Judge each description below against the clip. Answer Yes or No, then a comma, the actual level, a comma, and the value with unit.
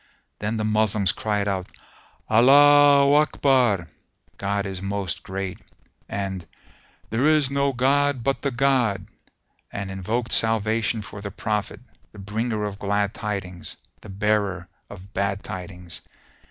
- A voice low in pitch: Yes, low, 105 Hz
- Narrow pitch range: No, average, 3.9 semitones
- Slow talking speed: Yes, slow, 125 wpm